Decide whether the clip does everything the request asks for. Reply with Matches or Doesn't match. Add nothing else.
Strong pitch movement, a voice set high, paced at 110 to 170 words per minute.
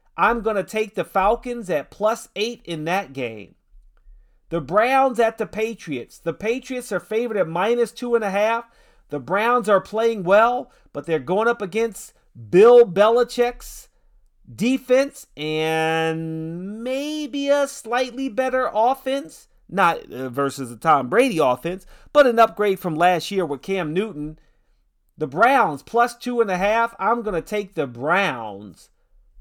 Matches